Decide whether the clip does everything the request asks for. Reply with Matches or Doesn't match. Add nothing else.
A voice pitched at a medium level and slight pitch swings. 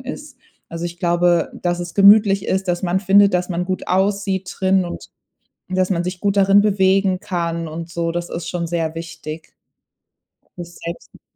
Matches